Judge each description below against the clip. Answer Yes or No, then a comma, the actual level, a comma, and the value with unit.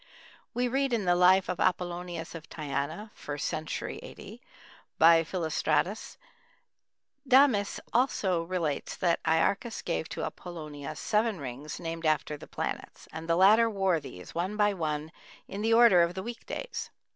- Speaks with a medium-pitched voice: Yes, medium, 175 Hz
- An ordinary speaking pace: Yes, average, 145 wpm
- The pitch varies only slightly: No, average, 4.7 semitones